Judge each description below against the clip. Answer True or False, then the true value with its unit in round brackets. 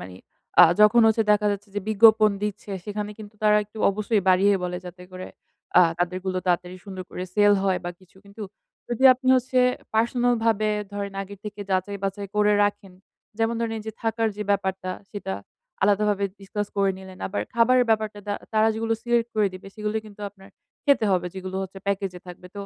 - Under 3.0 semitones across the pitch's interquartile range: True (2.4 semitones)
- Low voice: False (205 Hz)